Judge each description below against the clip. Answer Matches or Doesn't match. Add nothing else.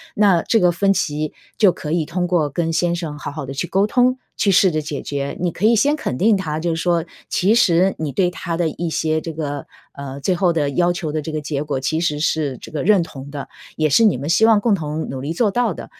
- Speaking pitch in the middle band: Matches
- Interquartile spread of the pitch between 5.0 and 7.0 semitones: Doesn't match